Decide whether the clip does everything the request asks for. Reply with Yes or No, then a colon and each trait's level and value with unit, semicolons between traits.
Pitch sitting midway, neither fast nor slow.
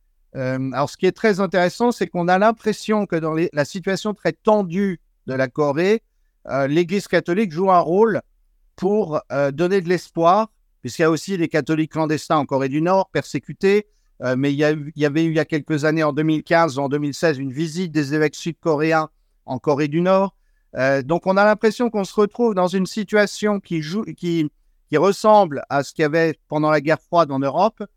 Yes: medium, 170 Hz; average, 210 wpm